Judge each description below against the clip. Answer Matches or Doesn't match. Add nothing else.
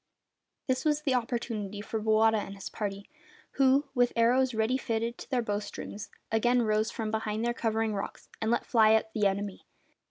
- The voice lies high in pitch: Matches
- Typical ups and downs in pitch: Doesn't match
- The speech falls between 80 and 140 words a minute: Doesn't match